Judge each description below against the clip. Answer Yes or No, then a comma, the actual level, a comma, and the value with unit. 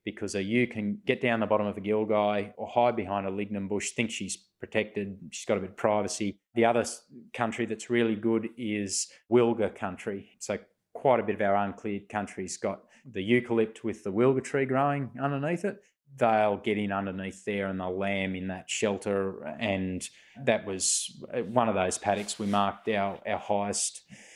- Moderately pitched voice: No, low, 105 Hz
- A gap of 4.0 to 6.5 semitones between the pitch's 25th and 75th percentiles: No, average, 2.7 semitones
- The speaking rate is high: No, average, 185 wpm